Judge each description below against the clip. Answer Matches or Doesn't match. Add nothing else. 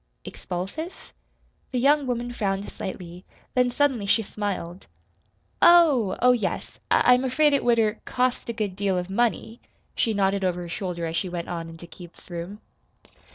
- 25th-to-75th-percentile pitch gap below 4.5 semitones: Doesn't match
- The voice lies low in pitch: Doesn't match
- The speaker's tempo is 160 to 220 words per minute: Matches